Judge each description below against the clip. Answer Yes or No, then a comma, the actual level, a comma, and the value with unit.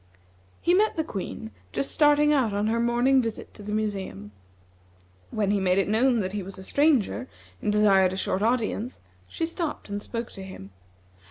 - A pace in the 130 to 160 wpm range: No, average, 185 wpm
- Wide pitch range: No, average, 4.9 semitones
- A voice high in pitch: Yes, high, 215 Hz